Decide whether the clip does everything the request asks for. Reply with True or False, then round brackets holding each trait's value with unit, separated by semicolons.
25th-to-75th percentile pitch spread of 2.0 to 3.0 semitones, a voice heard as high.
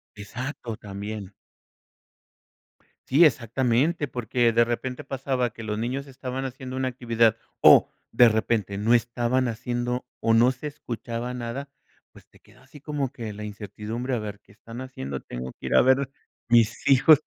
False (2.7 semitones; 120 Hz)